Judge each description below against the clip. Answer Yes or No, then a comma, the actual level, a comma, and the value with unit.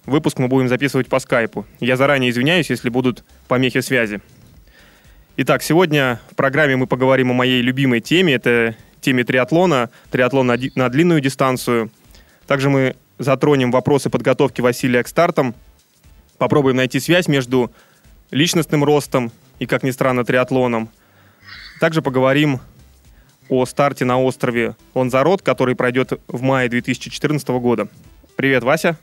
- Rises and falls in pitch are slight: Yes, narrow, 2.2 semitones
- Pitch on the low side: Yes, low, 130 Hz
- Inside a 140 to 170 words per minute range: No, average, 130 wpm